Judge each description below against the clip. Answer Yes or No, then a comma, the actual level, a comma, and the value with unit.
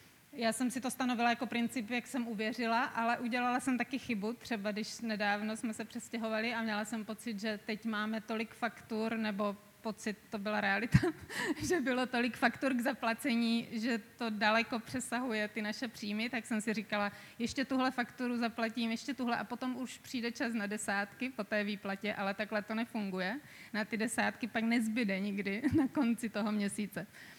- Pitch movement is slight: Yes, narrow, 2.2 semitones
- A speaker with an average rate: No, fast, 180 wpm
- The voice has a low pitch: No, high, 230 Hz